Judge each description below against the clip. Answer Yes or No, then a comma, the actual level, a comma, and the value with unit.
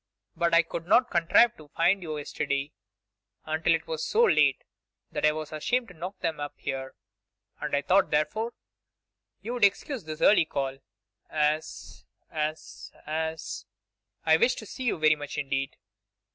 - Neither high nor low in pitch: Yes, medium, 160 Hz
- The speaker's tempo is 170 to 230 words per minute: No, average, 160 wpm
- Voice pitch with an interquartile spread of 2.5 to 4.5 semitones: Yes, average, 4.1 semitones